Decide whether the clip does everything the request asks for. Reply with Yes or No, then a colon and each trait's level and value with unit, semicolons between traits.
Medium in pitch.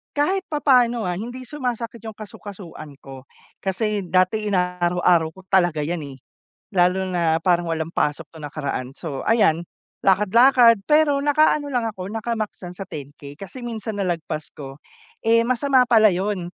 No: high, 195 Hz